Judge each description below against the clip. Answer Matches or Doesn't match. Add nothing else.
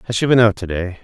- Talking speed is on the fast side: Matches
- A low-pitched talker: Matches